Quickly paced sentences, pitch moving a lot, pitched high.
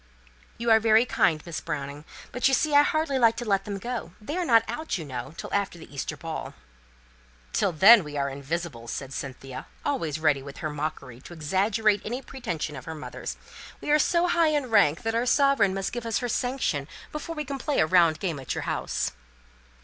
Yes: fast, 210 wpm; wide, 8.6 semitones; high, 195 Hz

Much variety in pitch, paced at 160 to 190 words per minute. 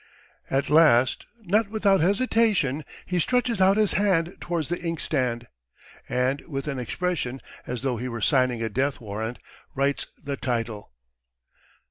No: wide, 6.5 semitones; average, 140 wpm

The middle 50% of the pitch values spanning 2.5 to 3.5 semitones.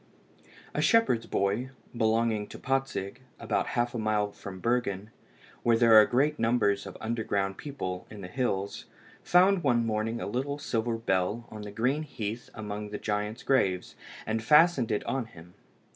Yes: average, 3.2 semitones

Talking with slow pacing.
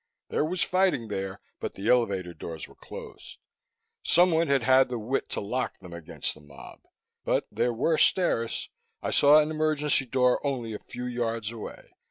No: average, 175 wpm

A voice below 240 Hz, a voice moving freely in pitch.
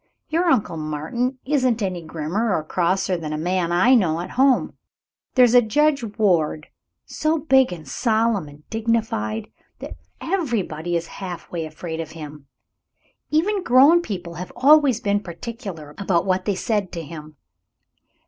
Yes: high, 190 Hz; wide, 7.2 semitones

